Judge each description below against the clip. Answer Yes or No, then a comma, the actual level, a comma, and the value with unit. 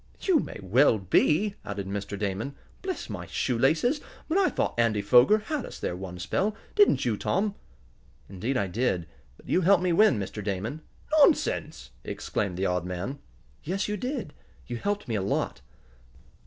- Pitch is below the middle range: Yes, low, 120 Hz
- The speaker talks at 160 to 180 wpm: Yes, average, 170 wpm